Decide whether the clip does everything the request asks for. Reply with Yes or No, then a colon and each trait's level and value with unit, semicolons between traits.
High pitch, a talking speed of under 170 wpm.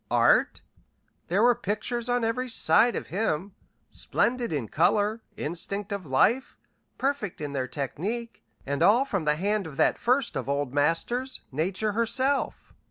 Yes: high, 205 Hz; average, 150 wpm